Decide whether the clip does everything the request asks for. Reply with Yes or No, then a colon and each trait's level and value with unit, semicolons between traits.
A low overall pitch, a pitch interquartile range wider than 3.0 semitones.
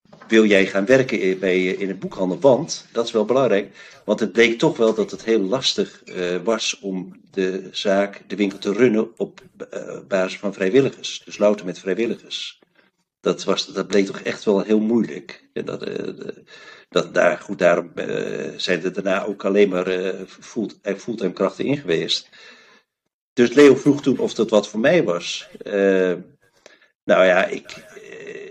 Yes: low, 100 Hz; average, 3.5 semitones